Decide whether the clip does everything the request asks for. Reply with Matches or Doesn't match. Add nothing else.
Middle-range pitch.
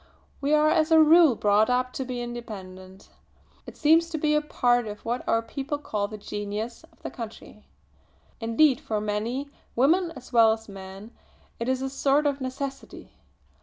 Doesn't match